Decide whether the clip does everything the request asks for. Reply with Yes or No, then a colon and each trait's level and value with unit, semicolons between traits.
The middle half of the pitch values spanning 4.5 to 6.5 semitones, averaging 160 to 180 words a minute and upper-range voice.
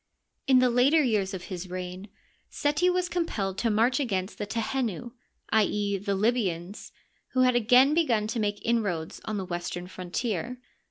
Yes: average, 4.8 semitones; average, 170 wpm; high, 215 Hz